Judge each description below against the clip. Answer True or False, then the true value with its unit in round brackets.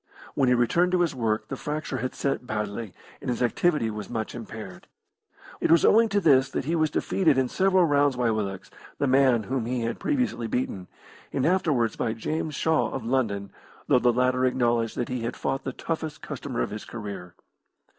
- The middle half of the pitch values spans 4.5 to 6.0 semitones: True (4.9 semitones)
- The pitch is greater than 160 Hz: False (125 Hz)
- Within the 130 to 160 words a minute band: False (195 wpm)